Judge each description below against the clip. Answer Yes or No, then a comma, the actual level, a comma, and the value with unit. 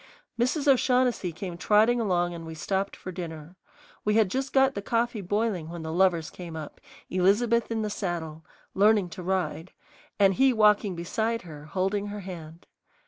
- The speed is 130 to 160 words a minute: No, average, 170 wpm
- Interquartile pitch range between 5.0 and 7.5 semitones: No, average, 4.4 semitones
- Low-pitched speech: No, high, 190 Hz